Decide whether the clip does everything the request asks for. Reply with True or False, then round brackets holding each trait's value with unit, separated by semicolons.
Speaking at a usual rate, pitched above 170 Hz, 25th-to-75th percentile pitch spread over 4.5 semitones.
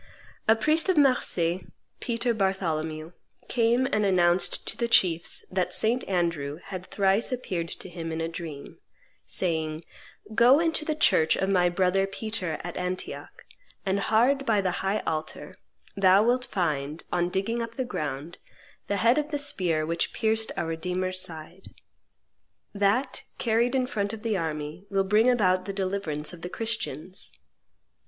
True (155 wpm; 190 Hz; 5.2 semitones)